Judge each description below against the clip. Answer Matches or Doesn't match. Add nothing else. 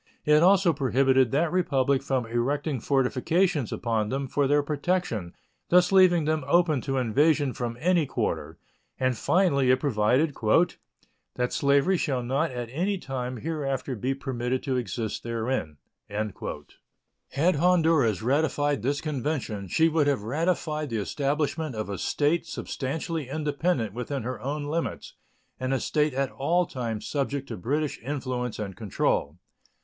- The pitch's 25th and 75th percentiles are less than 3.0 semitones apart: Doesn't match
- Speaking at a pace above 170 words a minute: Doesn't match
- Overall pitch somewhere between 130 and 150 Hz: Matches